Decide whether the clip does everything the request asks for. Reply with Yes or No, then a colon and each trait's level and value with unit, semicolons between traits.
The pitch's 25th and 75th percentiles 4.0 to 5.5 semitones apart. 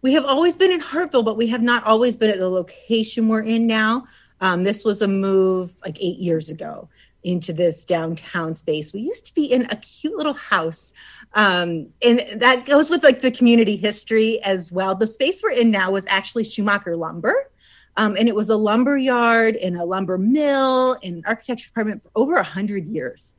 Yes: average, 4.7 semitones